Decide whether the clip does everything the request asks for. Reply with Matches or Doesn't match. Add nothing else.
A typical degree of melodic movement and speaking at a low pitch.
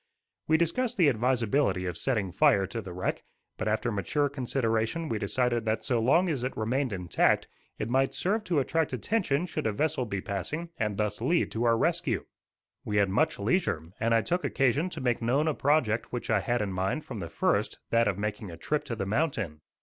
Doesn't match